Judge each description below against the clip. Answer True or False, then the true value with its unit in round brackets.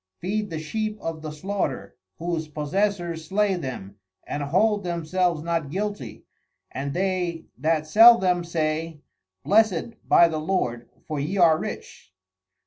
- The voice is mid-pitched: True (170 Hz)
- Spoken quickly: False (135 wpm)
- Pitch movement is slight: False (3.8 semitones)